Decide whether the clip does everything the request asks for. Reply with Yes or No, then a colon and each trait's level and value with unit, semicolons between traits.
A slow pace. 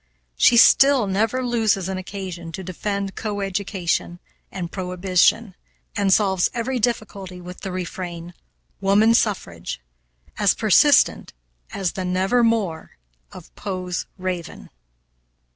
Yes: slow, 115 wpm